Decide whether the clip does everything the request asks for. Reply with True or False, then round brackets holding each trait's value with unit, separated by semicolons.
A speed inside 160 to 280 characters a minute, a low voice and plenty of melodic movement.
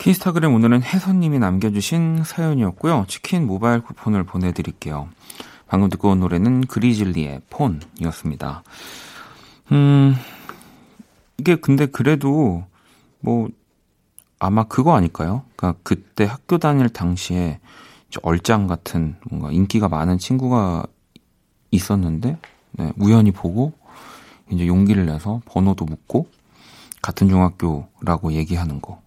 True (275 characters per minute; 100 Hz; 7.0 semitones)